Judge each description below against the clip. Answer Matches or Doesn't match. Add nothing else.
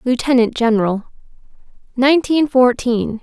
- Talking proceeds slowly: Matches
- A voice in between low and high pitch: Doesn't match